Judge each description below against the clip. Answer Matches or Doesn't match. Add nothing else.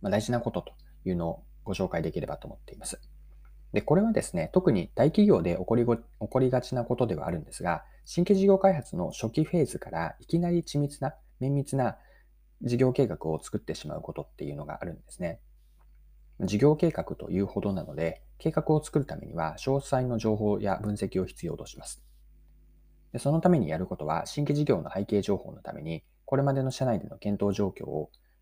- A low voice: Matches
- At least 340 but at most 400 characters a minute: Matches